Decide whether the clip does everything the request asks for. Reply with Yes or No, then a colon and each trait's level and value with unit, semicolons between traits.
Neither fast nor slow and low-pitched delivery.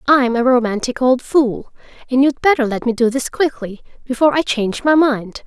No: average, 195 wpm; very high, 255 Hz